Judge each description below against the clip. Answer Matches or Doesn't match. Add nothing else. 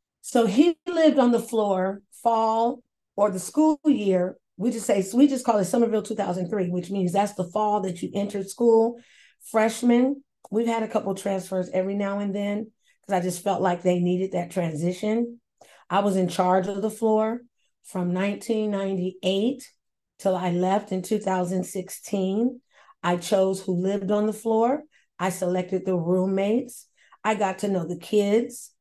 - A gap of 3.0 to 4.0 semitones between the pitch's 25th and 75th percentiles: Matches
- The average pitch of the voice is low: Doesn't match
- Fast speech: Doesn't match